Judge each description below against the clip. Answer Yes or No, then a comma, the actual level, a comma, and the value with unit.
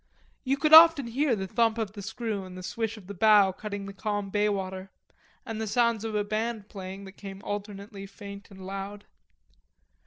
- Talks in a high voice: Yes, high, 205 Hz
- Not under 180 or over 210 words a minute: Yes, average, 190 wpm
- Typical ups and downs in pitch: No, narrow, 2.3 semitones